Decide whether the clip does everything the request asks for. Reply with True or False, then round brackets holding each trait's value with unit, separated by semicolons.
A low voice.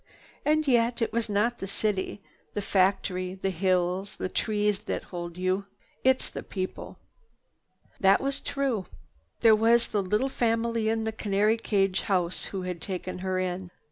False (200 Hz)